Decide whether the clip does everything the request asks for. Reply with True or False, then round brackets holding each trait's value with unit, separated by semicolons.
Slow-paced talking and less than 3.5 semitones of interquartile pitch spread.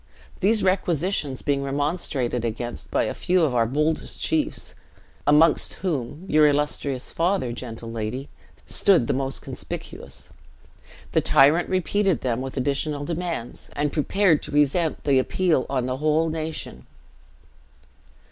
False (130 wpm; 4.3 semitones)